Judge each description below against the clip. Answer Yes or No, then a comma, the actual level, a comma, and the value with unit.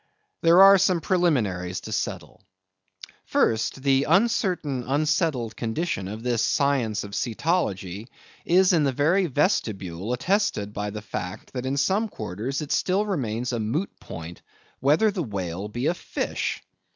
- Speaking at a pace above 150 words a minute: No, average, 145 wpm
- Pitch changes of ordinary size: No, wide, 8.3 semitones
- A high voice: No, low, 135 Hz